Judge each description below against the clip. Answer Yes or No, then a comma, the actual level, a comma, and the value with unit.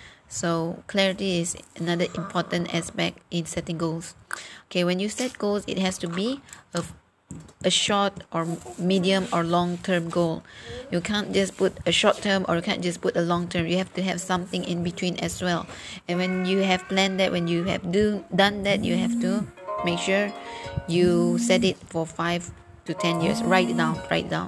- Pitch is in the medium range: Yes, medium, 180 Hz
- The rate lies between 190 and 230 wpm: Yes, average, 195 wpm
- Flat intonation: Yes, narrow, 2.1 semitones